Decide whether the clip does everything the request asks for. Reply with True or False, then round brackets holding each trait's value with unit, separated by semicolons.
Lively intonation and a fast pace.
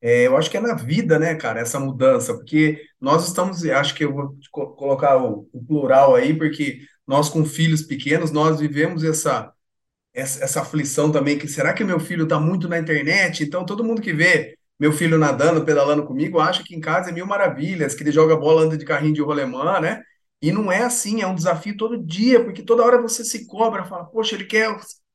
False (5.0 semitones; 215 wpm)